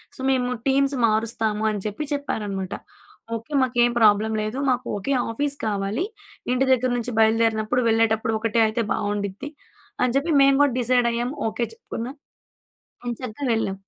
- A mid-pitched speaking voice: No, high, 230 Hz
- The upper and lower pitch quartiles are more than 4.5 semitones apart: No, average, 2.9 semitones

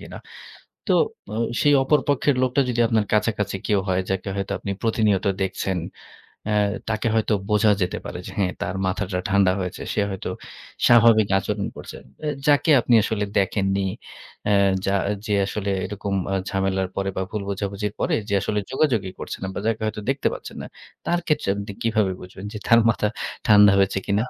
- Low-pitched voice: Yes, low, 105 Hz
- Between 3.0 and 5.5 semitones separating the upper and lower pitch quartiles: No, narrow, 2.4 semitones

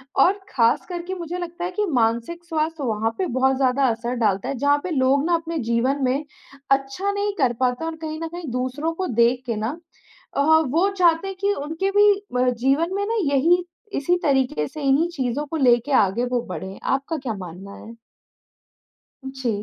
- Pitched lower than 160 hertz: No, very high, 275 Hz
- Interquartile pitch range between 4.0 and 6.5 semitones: Yes, average, 5.3 semitones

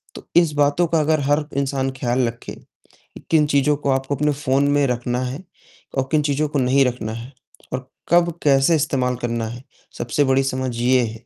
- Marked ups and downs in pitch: No, narrow, 2.6 semitones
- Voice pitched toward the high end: No, low, 135 Hz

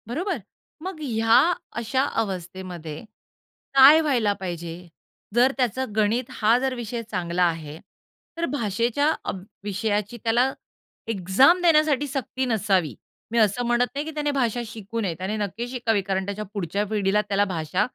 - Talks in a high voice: Yes, high, 220 Hz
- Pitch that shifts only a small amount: No, average, 5.0 semitones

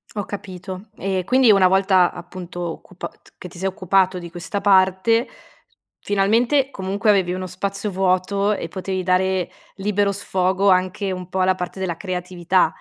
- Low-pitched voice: No, high, 190 Hz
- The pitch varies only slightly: Yes, narrow, 1.5 semitones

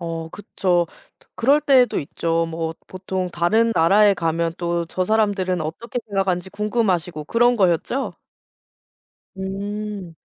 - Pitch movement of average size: Yes, average, 3.9 semitones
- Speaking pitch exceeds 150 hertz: Yes, medium, 185 Hz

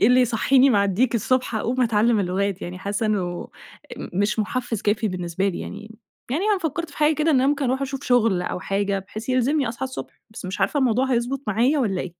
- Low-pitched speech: No, high, 230 Hz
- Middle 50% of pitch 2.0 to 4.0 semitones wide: No, average, 4.6 semitones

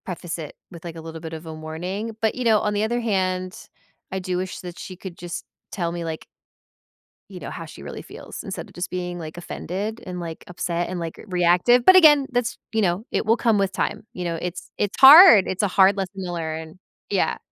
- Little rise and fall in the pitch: No, average, 3.5 semitones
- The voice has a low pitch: No, medium, 185 Hz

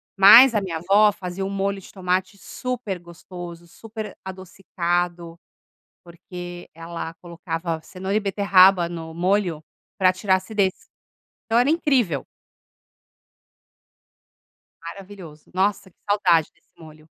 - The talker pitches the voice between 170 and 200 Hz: Yes, medium, 185 Hz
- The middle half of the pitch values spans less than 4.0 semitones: Yes, average, 2.7 semitones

